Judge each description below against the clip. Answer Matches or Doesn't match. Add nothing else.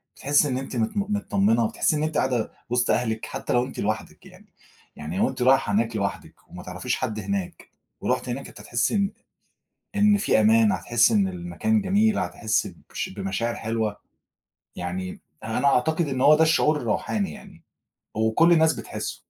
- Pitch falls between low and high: Doesn't match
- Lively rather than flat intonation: Matches